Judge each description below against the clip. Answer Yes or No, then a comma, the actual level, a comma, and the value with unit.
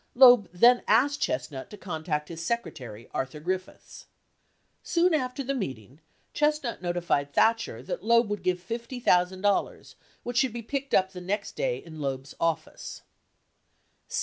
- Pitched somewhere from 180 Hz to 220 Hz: Yes, high, 190 Hz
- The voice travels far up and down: Yes, wide, 7.4 semitones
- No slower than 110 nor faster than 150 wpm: Yes, average, 140 wpm